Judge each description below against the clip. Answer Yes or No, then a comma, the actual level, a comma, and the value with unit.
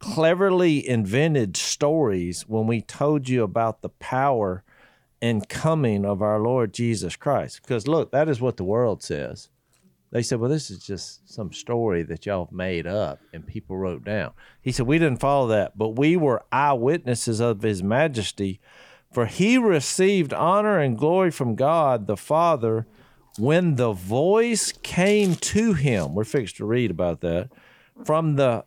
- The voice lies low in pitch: Yes, low, 120 Hz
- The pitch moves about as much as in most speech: No, wide, 6.7 semitones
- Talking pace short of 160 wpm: No, average, 165 wpm